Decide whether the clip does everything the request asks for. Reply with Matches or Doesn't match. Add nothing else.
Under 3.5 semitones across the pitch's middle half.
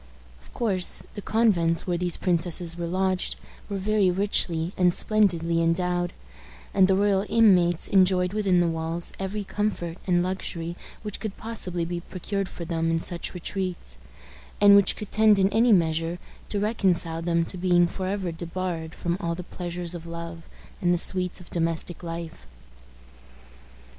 Matches